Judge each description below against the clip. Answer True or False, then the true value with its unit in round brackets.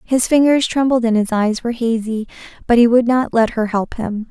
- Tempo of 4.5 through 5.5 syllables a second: True (5.3 syllables/s)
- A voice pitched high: True (235 Hz)